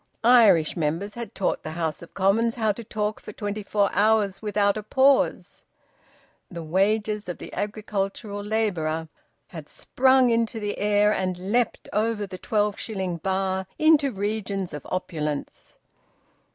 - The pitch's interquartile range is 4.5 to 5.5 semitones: No, average, 2.7 semitones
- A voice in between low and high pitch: No, high, 205 Hz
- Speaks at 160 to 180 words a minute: No, average, 145 wpm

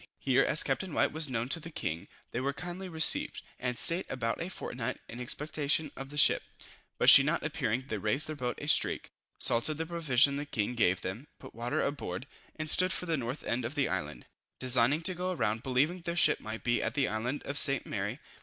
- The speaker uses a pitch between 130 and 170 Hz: Yes, low, 135 Hz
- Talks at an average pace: No, fast, 220 wpm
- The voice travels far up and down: No, average, 4.7 semitones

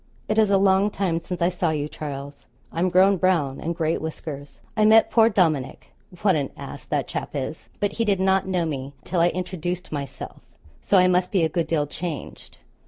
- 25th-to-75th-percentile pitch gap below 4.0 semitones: Yes, average, 3.6 semitones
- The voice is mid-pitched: Yes, medium, 175 Hz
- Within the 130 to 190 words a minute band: No, fast, 205 wpm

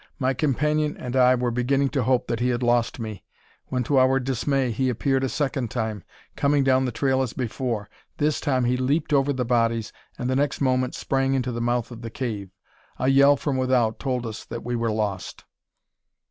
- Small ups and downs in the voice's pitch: Yes, narrow, 2.2 semitones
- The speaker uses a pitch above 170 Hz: No, low, 130 Hz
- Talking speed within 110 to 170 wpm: No, fast, 205 wpm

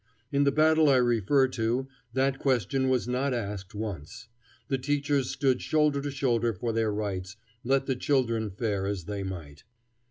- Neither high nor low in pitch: No, low, 125 Hz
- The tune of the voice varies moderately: Yes, average, 4.7 semitones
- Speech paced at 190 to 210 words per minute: No, average, 165 wpm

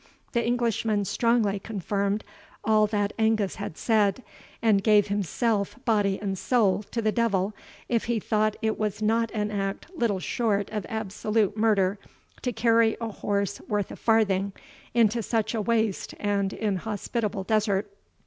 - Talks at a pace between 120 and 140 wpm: No, average, 150 wpm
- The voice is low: No, high, 215 Hz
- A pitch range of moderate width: No, narrow, 2.0 semitones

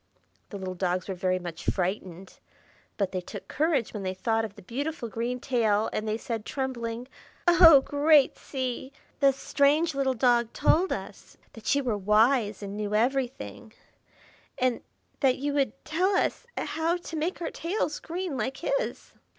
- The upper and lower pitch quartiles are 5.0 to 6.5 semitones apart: Yes, wide, 5.5 semitones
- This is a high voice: Yes, very high, 250 Hz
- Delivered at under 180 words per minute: Yes, average, 165 wpm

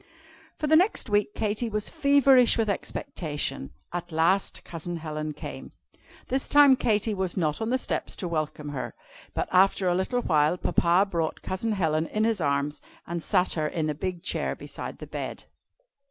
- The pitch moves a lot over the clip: Yes, wide, 5.8 semitones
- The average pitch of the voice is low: No, medium, 185 Hz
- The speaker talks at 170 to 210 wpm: Yes, average, 175 wpm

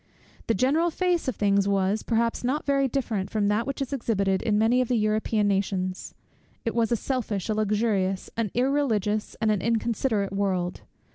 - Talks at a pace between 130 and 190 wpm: Yes, average, 180 wpm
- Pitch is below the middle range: No, high, 220 Hz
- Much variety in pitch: No, average, 3.7 semitones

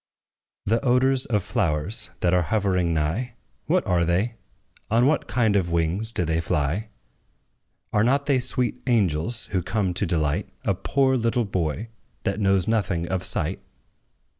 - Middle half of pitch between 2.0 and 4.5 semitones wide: No, average, 5.3 semitones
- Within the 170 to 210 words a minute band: No, average, 155 wpm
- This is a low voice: Yes, low, 100 Hz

